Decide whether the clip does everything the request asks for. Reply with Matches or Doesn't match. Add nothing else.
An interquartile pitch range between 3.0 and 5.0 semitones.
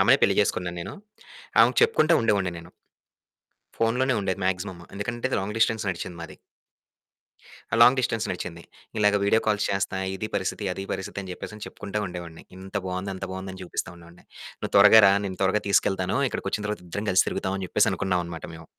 Doesn't match